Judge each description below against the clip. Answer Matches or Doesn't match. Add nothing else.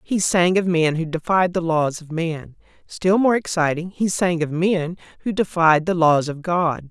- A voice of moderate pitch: Matches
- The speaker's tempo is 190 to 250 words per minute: Matches